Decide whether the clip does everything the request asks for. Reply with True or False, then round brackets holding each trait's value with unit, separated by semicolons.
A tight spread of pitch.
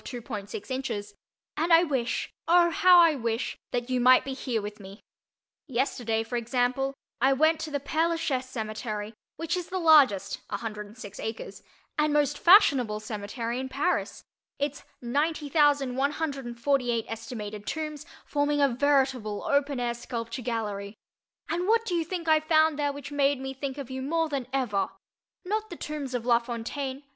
False (4.4 semitones)